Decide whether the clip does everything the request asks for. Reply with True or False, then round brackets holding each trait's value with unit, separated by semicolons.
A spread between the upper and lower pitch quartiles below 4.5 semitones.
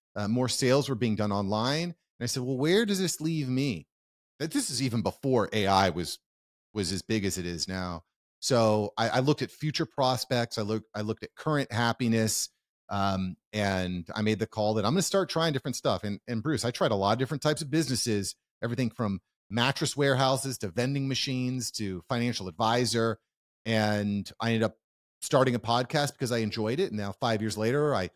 True (4.1 semitones)